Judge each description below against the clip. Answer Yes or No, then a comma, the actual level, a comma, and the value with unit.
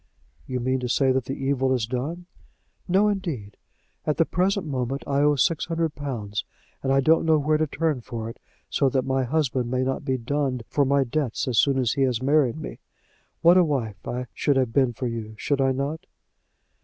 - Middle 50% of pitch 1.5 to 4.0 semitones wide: Yes, average, 3.2 semitones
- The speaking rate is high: Yes, fast, 210 wpm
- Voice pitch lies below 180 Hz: Yes, low, 135 Hz